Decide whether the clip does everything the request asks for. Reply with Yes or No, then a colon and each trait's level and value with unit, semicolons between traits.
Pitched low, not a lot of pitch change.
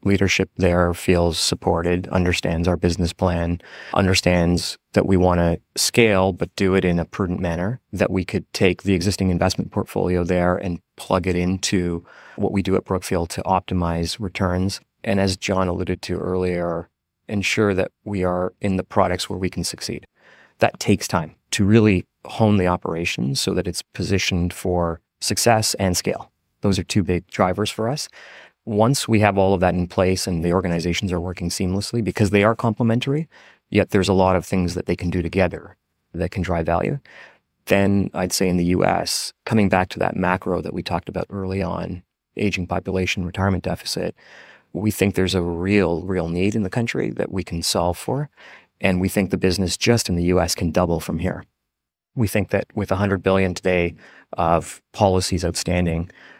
Yes: very low, 95 Hz; narrow, 2.0 semitones